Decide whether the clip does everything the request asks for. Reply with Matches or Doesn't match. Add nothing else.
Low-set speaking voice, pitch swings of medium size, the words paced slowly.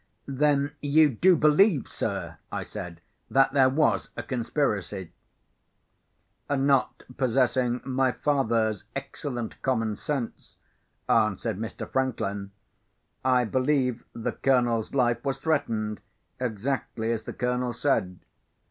Matches